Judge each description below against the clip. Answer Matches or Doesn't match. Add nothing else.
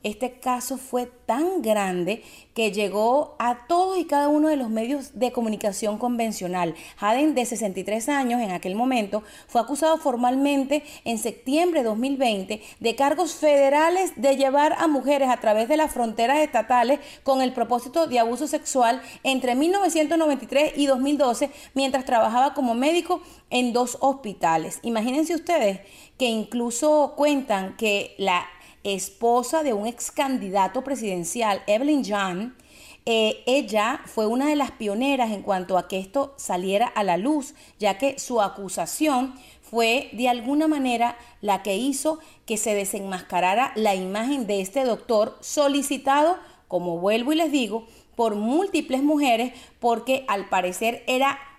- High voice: Matches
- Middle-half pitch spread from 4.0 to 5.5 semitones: Matches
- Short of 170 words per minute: Matches